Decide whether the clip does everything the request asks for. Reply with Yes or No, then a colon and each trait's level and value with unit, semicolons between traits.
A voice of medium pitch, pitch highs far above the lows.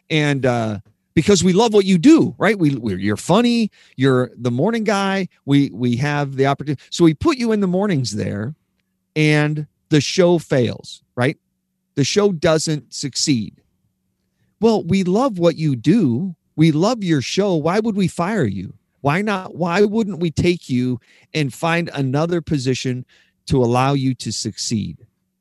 Yes: medium, 155 Hz; wide, 6.5 semitones